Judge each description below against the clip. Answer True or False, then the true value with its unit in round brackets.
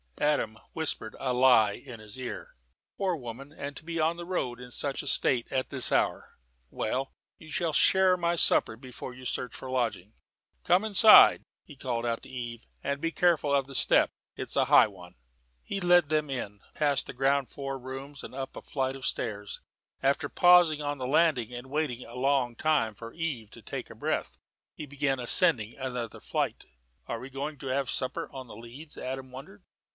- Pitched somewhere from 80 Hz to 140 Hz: True (135 Hz)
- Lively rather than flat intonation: False (3.5 semitones)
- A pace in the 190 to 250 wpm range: True (195 wpm)